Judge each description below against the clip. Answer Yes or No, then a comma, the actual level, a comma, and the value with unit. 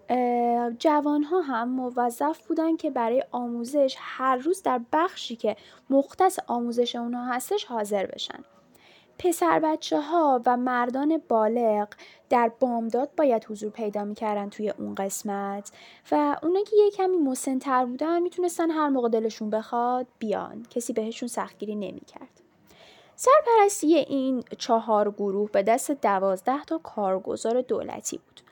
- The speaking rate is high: No, average, 130 wpm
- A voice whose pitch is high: Yes, high, 245 Hz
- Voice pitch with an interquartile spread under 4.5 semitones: No, average, 5.1 semitones